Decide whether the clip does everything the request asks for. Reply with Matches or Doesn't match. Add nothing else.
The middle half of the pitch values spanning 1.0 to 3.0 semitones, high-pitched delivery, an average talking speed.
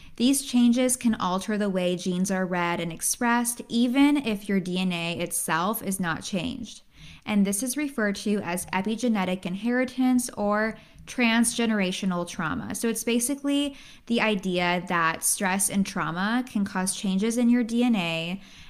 Doesn't match